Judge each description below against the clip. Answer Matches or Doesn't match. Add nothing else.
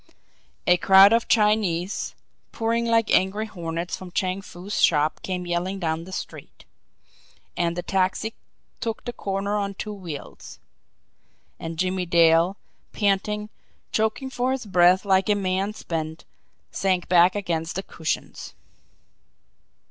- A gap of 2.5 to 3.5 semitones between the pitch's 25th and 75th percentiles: Matches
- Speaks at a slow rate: Matches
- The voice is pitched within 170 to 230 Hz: Matches